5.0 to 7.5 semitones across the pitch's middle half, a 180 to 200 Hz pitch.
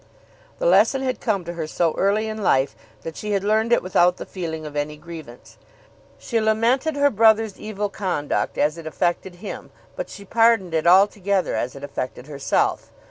Yes: average, 5.3 semitones; high, 190 Hz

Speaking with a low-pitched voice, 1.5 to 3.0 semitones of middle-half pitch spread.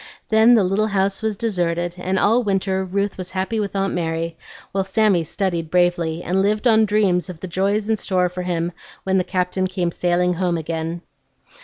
No: medium, 185 Hz; narrow, 2.4 semitones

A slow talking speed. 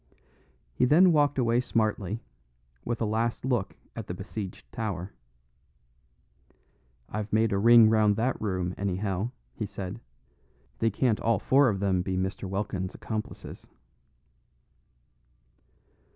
Yes: slow, 125 wpm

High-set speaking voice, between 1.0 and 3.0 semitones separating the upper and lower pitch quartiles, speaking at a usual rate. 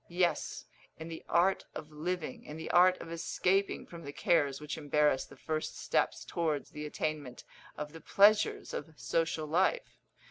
No: medium, 160 Hz; average, 2.7 semitones; average, 165 wpm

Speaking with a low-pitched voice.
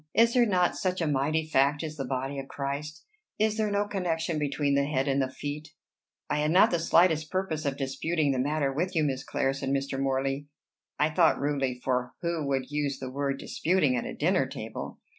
No: medium, 145 Hz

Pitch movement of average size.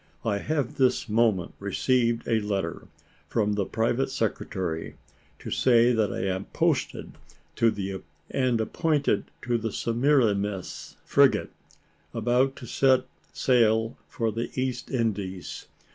Yes: average, 3.5 semitones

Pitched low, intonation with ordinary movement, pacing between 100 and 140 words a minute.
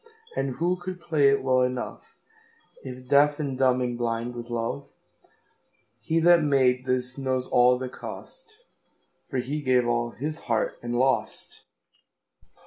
Yes: low, 130 Hz; average, 3.4 semitones; slow, 135 wpm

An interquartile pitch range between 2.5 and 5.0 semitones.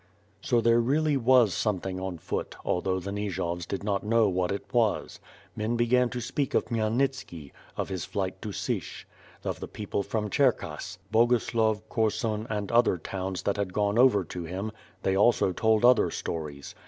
Yes: average, 3.7 semitones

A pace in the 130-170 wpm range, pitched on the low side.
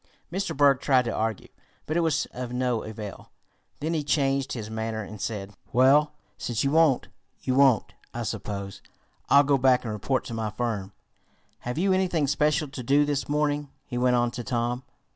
No: average, 185 wpm; low, 130 Hz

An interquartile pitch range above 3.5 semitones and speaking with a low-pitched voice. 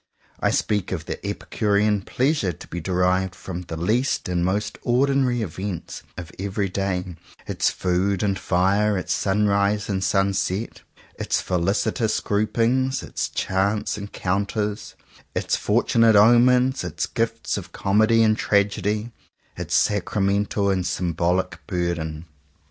No: average, 2.8 semitones; low, 100 Hz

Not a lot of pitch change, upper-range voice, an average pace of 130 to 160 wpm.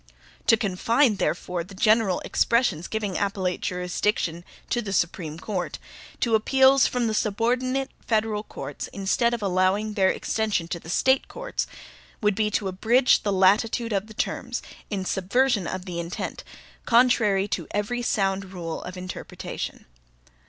No: average, 3.7 semitones; high, 205 Hz; average, 145 wpm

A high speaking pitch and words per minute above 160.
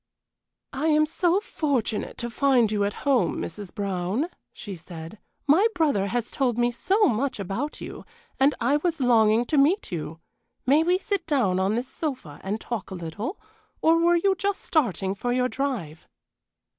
Yes: high, 245 Hz; average, 170 wpm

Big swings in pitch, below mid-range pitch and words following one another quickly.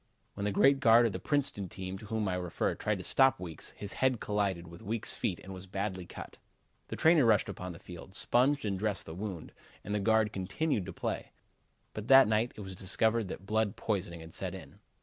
No: average, 3.3 semitones; low, 100 Hz; fast, 220 wpm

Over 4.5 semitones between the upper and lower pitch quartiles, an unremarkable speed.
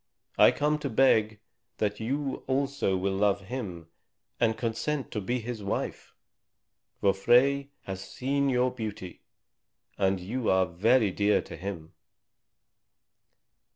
No: average, 5.1 semitones; slow, 125 wpm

